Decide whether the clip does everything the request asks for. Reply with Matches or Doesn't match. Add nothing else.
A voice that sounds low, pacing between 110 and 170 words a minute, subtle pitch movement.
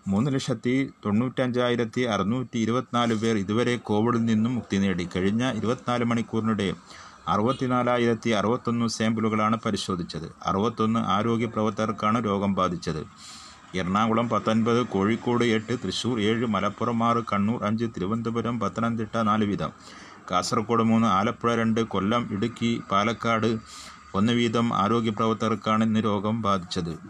Matches